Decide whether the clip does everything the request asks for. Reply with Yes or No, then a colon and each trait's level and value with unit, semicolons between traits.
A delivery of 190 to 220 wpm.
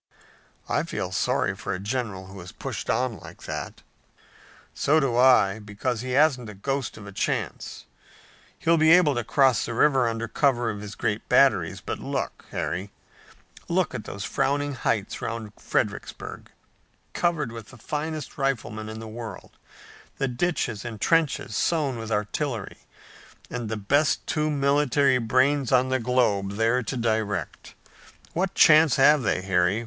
No: average, 155 wpm